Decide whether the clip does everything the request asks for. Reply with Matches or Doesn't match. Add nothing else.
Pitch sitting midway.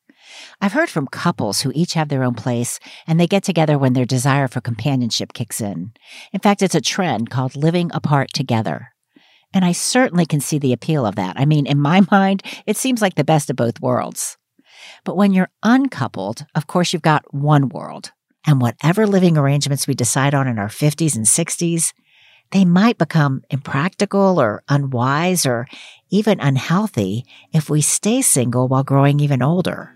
Matches